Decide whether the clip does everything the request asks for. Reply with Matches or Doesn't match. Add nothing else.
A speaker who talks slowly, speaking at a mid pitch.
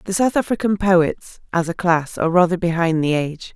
Doesn't match